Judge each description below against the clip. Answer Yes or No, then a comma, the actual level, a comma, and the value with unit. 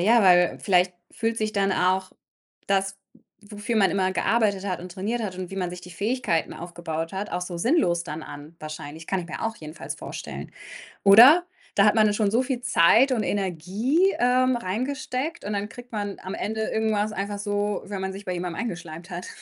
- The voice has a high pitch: Yes, high, 200 Hz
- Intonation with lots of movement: No, average, 3.8 semitones